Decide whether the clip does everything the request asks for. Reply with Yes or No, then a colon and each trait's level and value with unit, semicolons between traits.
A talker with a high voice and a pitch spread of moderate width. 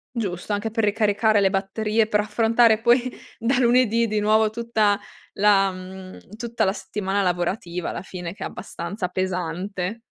Yes: high, 210 Hz; average, 3.0 semitones